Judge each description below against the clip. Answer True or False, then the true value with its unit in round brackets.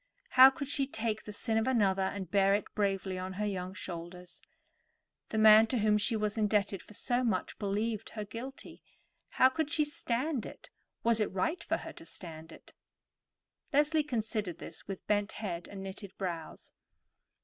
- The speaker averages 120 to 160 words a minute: False (175 wpm)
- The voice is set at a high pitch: True (210 Hz)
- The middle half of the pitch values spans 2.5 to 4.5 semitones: True (3.6 semitones)